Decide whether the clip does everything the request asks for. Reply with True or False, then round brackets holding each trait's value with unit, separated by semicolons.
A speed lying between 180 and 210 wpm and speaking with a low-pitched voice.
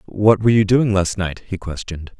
False (220 wpm; 100 Hz)